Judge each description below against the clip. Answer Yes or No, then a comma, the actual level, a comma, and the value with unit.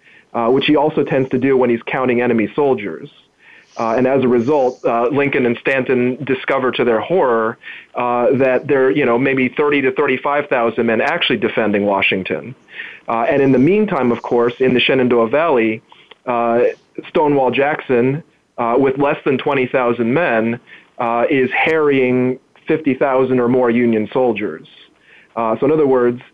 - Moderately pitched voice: No, low, 125 Hz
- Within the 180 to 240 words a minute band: No, average, 170 wpm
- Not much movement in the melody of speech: Yes, narrow, 2.3 semitones